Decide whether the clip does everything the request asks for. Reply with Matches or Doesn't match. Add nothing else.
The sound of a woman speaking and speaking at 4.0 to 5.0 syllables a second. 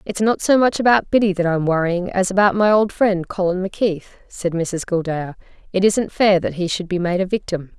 Doesn't match